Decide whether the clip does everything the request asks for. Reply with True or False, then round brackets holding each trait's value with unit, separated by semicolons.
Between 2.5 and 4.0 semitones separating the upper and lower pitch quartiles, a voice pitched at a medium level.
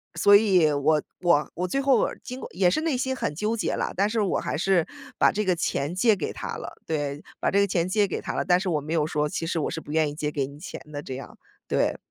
False (5.1 semitones; 175 Hz)